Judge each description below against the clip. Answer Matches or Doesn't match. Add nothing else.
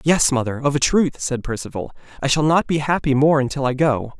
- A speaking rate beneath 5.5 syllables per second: Doesn't match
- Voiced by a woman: Doesn't match